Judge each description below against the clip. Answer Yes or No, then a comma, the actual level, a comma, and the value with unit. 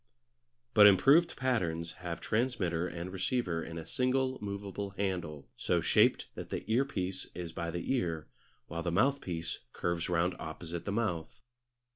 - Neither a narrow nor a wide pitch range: Yes, average, 4.8 semitones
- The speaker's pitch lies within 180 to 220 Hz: No, very low, 90 Hz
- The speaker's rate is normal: Yes, average, 145 wpm